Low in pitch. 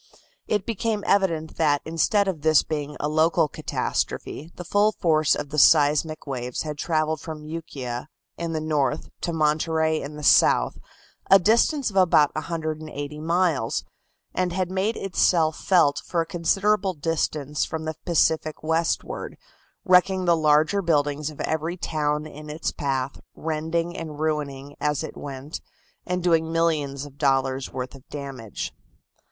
No: medium, 155 Hz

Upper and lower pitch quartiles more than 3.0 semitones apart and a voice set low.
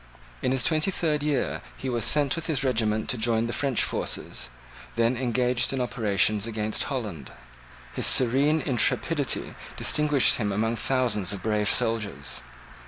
Yes: average, 3.9 semitones; low, 120 Hz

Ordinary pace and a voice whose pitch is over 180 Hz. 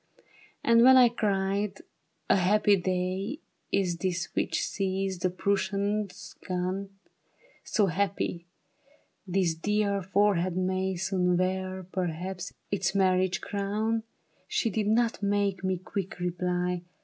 No: slow, 120 wpm; high, 190 Hz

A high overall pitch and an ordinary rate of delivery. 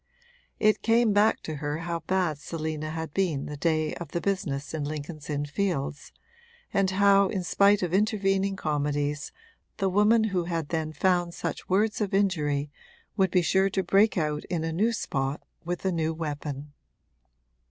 No: medium, 170 Hz; average, 170 wpm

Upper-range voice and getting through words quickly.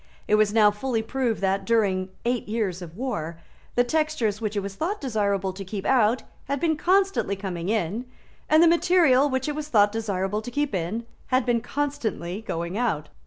No: high, 220 Hz; average, 190 wpm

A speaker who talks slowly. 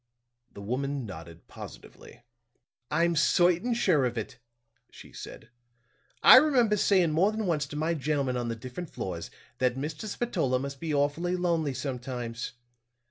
No: average, 145 wpm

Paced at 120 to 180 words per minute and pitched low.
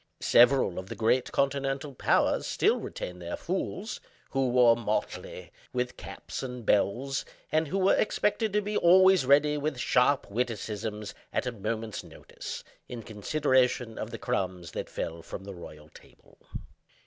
Yes: average, 150 wpm; low, 125 Hz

